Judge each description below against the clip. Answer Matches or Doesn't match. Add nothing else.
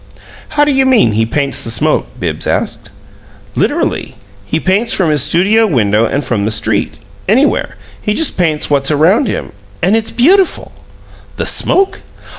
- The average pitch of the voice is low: Doesn't match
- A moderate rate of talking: Matches